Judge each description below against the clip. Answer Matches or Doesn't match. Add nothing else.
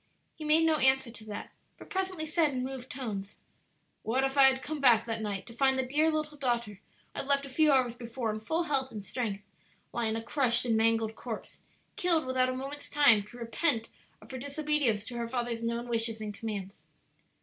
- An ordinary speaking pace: Doesn't match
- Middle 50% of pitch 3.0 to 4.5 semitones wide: Matches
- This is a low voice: Doesn't match